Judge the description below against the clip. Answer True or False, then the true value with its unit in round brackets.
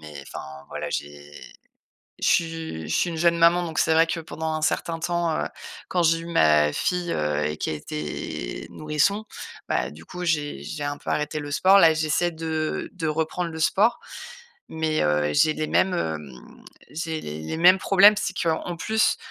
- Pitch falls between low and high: True (160 Hz)